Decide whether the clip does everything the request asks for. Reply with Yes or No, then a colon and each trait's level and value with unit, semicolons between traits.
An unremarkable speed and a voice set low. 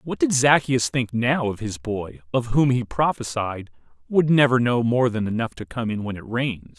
No: fast, 210 wpm; low, 120 Hz